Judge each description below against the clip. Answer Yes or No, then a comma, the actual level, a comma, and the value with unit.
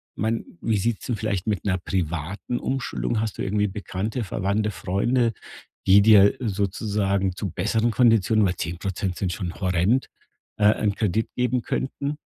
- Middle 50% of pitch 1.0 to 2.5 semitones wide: No, average, 2.9 semitones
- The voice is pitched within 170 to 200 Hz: No, low, 105 Hz